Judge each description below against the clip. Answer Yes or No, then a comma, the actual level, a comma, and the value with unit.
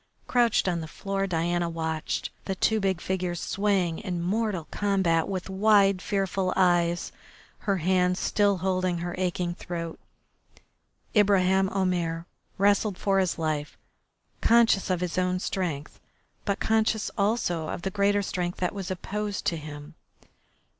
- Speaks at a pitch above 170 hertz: Yes, medium, 185 Hz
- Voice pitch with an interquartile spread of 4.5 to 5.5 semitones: No, narrow, 2.4 semitones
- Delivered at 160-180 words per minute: No, average, 140 wpm